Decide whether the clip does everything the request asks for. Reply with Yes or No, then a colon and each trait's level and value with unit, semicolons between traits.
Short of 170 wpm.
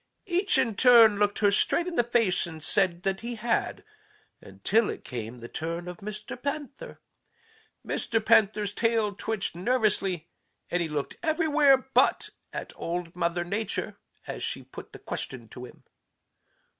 Yes: average, 155 wpm